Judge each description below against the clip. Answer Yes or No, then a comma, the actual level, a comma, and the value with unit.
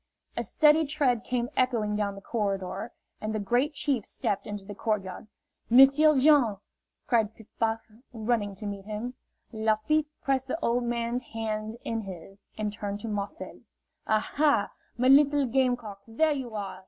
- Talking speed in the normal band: Yes, average, 165 wpm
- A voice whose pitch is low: No, high, 225 Hz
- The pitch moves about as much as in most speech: Yes, average, 3.9 semitones